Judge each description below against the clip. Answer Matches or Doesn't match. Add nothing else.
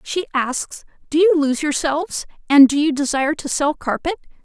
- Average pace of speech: Matches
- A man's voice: Doesn't match